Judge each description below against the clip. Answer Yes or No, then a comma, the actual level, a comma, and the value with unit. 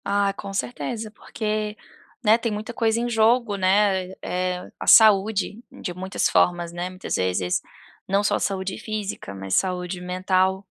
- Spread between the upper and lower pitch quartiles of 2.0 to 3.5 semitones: Yes, average, 2.8 semitones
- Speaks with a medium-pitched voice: No, high, 195 Hz